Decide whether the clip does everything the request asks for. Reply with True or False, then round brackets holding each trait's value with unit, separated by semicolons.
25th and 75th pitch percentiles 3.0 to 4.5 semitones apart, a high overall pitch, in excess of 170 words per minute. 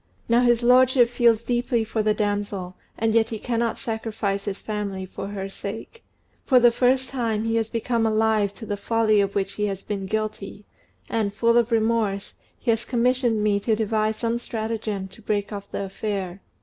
False (2.4 semitones; 220 Hz; 190 wpm)